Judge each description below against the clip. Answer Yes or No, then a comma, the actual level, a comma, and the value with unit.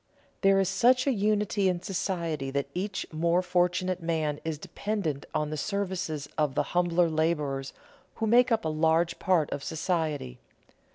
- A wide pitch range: No, average, 3.9 semitones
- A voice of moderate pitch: Yes, medium, 170 Hz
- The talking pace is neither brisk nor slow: Yes, average, 160 wpm